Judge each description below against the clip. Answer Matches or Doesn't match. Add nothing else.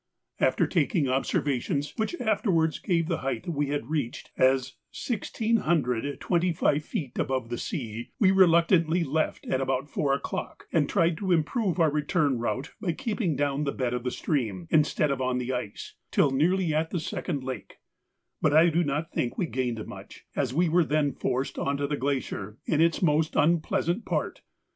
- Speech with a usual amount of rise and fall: Matches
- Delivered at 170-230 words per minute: Matches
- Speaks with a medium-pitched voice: Matches